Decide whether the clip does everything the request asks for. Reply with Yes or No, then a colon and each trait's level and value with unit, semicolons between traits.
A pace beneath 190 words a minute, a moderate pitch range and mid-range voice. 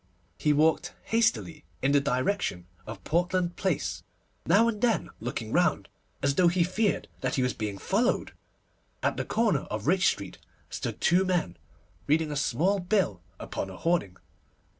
No: average, 160 wpm; wide, 6.6 semitones; medium, 165 Hz